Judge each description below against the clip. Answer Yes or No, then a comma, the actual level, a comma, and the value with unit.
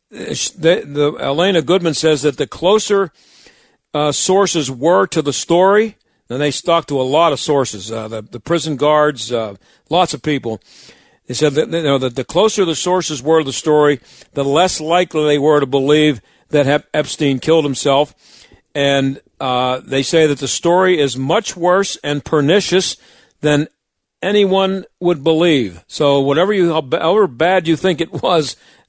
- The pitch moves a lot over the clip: No, average, 3.7 semitones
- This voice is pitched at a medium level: Yes, medium, 150 Hz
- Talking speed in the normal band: Yes, average, 170 wpm